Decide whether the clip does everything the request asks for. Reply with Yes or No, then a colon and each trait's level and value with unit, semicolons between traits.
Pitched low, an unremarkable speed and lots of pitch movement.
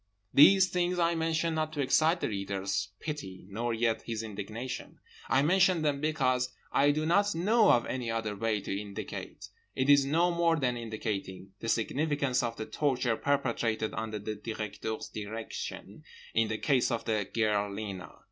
Yes: low, 120 Hz; average, 160 wpm; wide, 6.1 semitones